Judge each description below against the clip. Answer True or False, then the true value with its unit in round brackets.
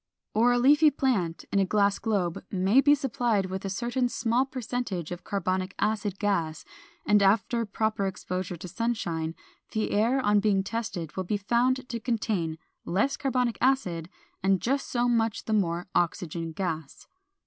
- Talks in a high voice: True (205 Hz)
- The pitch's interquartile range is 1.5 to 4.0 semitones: False (4.6 semitones)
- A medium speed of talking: True (160 wpm)